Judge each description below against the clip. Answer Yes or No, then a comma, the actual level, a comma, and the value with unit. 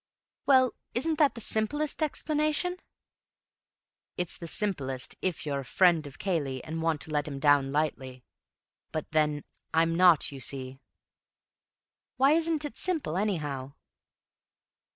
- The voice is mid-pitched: Yes, medium, 165 Hz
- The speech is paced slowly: Yes, slow, 130 wpm